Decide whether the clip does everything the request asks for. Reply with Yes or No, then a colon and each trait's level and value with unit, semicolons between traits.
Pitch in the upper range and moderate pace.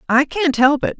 No: very high, 290 Hz; fast, 240 wpm